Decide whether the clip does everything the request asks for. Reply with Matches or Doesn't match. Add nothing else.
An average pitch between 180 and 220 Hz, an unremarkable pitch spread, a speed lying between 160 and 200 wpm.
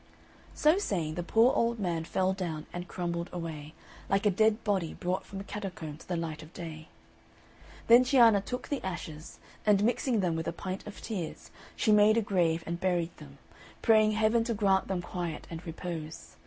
Matches